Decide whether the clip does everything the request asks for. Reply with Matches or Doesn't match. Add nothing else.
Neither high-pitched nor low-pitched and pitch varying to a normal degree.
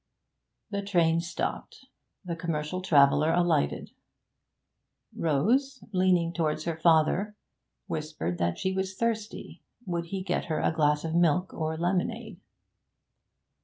Matches